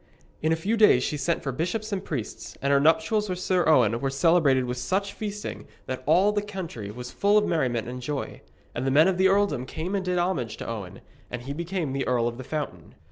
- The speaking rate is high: Yes, fast, 240 wpm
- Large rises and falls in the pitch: Yes, wide, 6.9 semitones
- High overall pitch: No, medium, 155 Hz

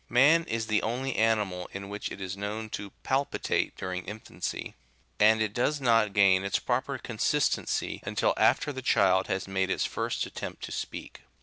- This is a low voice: Yes, low, 110 Hz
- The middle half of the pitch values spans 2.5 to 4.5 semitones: Yes, average, 4.0 semitones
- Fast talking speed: No, average, 180 wpm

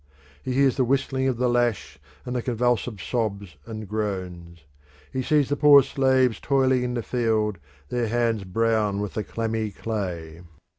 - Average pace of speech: Yes, average, 160 wpm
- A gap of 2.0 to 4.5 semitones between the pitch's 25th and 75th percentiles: Yes, average, 3.6 semitones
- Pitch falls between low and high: No, low, 115 Hz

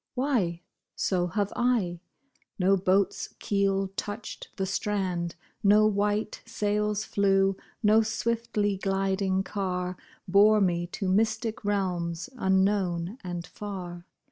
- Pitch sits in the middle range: No, high, 195 Hz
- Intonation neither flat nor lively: No, narrow, 2.3 semitones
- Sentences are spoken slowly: Yes, slow, 110 wpm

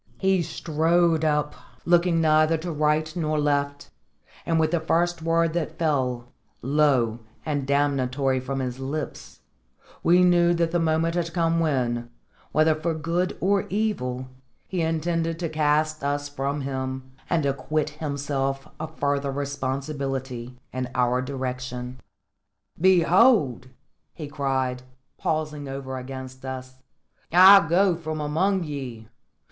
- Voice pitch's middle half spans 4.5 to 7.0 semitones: No, average, 3.7 semitones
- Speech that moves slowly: Yes, slow, 130 wpm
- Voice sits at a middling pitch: Yes, medium, 150 Hz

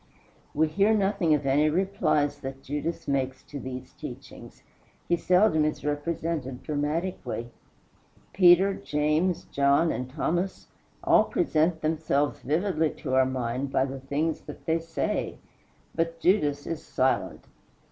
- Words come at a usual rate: No, slow, 130 wpm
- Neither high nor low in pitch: Yes, medium, 155 Hz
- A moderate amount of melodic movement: Yes, average, 3.4 semitones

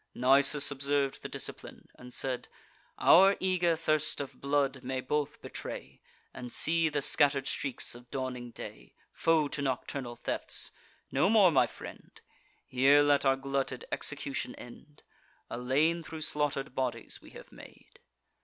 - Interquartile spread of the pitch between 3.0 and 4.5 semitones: No, narrow, 2.6 semitones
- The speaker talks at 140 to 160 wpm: Yes, average, 145 wpm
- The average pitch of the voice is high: No, medium, 140 Hz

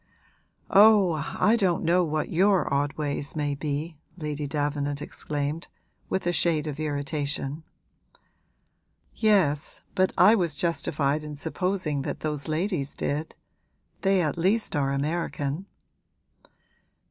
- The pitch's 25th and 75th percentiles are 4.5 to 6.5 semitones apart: No, average, 3.6 semitones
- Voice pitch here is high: No, medium, 155 Hz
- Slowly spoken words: Yes, slow, 120 wpm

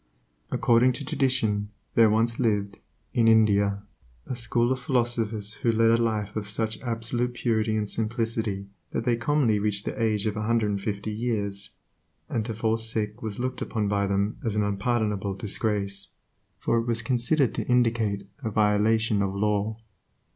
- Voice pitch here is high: No, low, 110 Hz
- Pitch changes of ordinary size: No, narrow, 2.1 semitones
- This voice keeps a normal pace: Yes, average, 170 wpm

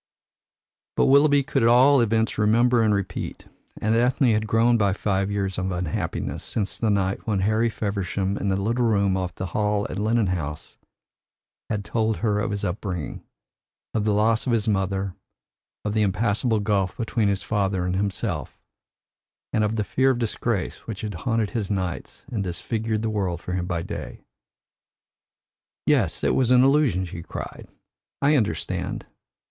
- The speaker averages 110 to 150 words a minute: No, average, 170 wpm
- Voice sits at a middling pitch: No, low, 105 Hz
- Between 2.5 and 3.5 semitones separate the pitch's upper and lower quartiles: Yes, average, 2.9 semitones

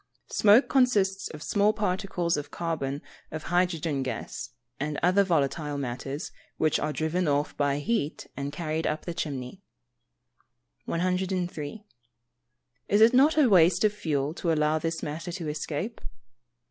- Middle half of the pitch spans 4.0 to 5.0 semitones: Yes, average, 4.4 semitones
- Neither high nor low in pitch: Yes, medium, 165 Hz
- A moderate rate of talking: Yes, average, 145 wpm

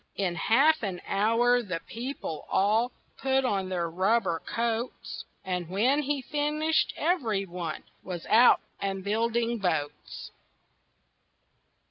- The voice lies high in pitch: Yes, high, 225 Hz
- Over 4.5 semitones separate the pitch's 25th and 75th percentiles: Yes, average, 5.1 semitones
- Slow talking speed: Yes, slow, 110 wpm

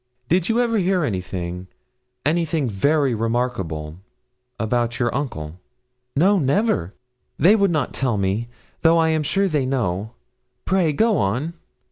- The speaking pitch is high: No, low, 135 Hz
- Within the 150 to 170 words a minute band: No, slow, 135 wpm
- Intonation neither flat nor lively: No, wide, 8.3 semitones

